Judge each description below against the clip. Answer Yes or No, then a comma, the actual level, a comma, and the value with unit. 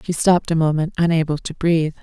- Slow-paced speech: No, fast, 205 wpm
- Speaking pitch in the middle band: Yes, medium, 165 Hz